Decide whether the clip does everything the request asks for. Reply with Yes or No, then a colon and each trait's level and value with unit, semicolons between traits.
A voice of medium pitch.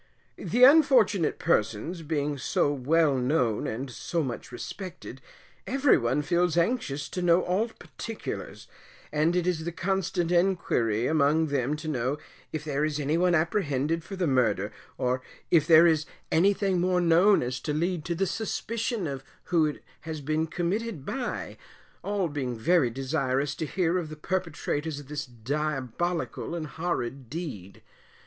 Yes: medium, 160 Hz